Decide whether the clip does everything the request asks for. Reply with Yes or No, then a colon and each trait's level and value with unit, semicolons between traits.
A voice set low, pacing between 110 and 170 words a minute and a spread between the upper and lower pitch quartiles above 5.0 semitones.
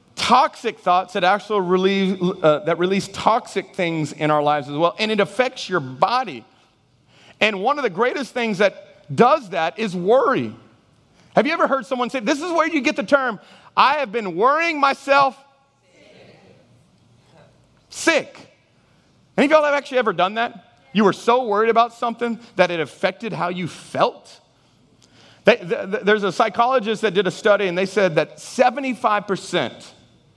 No: high, 210 Hz; average, 160 wpm; wide, 5.6 semitones